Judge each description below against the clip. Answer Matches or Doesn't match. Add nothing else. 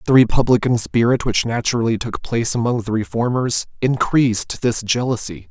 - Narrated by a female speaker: Doesn't match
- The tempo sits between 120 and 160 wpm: Matches